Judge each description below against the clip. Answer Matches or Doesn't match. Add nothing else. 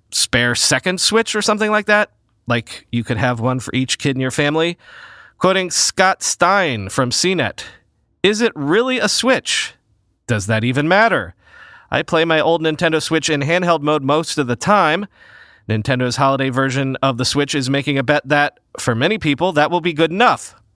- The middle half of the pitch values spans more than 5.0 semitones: Matches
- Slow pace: Doesn't match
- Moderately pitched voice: Matches